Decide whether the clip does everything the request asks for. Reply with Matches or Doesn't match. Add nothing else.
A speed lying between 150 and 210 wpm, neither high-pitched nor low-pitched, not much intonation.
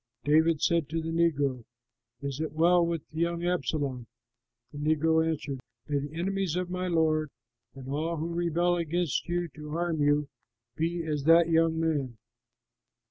Matches